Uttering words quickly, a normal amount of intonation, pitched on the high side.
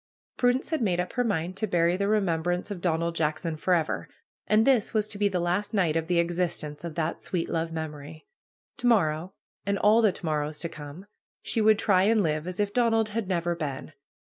No: fast, 210 wpm; average, 4.4 semitones; medium, 180 Hz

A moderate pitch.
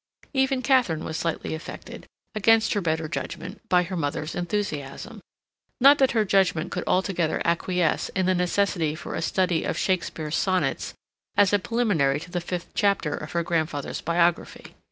Yes: medium, 180 Hz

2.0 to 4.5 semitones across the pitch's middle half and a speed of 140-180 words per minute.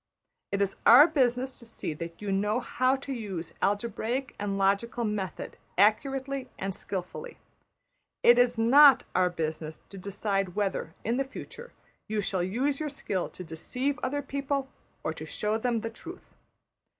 No: average, 5.3 semitones; average, 160 wpm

